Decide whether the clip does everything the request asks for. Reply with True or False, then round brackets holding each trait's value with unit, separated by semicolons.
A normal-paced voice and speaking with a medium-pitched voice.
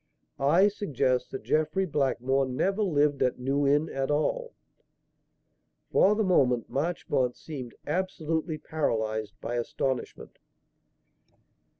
False (105 wpm; 145 Hz)